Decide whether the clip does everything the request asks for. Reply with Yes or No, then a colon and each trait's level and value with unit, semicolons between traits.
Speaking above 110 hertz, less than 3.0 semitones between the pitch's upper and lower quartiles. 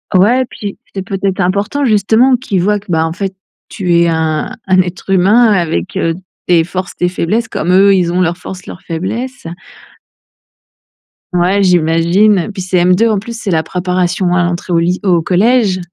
Yes: medium, 185 Hz; narrow, 2.6 semitones